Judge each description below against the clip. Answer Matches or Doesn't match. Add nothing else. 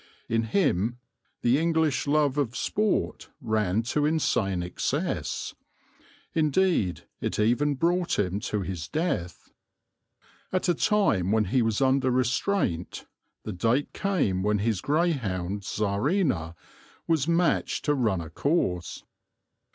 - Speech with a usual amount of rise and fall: Doesn't match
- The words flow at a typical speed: Doesn't match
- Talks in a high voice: Doesn't match